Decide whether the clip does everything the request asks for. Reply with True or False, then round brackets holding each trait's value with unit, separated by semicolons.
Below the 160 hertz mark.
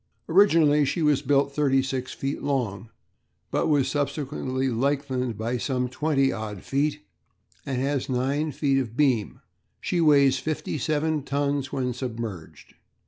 True (135 Hz)